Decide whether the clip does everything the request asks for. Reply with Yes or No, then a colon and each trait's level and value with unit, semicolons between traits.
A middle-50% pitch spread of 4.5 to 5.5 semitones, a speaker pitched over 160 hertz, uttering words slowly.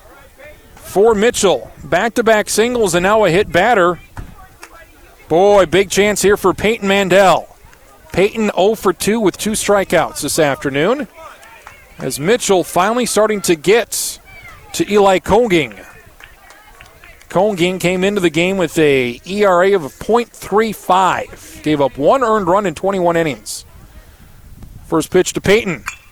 Yes: average, 5.1 semitones; medium, 185 Hz; slow, 130 wpm